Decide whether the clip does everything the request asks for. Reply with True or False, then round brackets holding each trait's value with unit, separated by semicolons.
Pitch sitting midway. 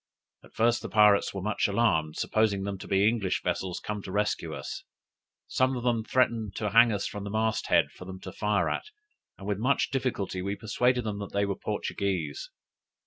False (105 Hz)